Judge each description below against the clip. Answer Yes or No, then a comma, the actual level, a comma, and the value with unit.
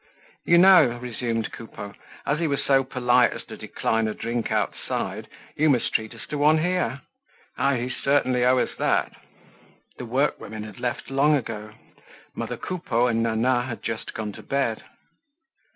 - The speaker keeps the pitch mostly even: No, average, 3.6 semitones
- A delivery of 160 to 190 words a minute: Yes, average, 165 wpm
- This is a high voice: No, low, 125 Hz